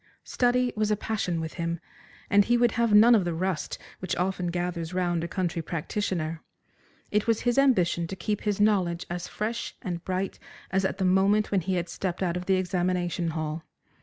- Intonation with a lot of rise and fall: No, average, 3.3 semitones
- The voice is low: No, medium, 185 Hz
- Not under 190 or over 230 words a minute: Yes, average, 195 wpm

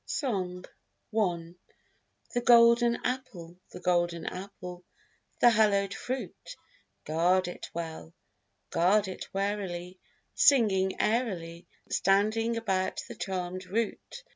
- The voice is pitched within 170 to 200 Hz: Yes, high, 190 Hz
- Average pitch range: Yes, average, 4.1 semitones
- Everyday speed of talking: No, slow, 100 wpm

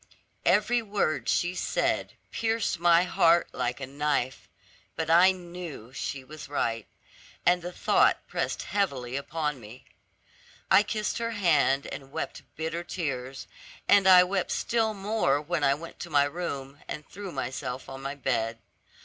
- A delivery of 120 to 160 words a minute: Yes, average, 150 wpm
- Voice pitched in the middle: Yes, medium, 160 Hz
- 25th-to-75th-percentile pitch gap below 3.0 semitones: No, average, 5.1 semitones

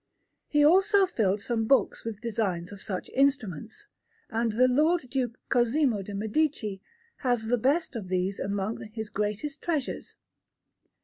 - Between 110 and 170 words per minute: Yes, average, 140 wpm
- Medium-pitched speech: No, high, 230 Hz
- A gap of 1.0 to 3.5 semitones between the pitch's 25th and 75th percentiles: No, wide, 5.4 semitones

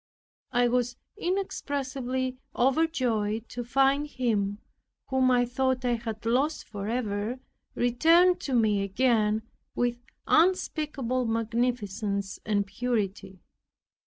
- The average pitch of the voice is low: No, high, 245 Hz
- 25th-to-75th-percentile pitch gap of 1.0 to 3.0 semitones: No, average, 3.4 semitones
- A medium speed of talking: No, slow, 100 wpm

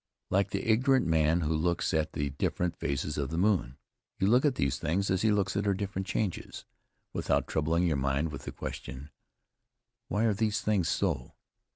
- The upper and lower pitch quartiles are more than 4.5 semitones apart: Yes, average, 5.0 semitones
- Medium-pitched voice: No, very low, 85 Hz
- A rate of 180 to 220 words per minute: Yes, average, 190 wpm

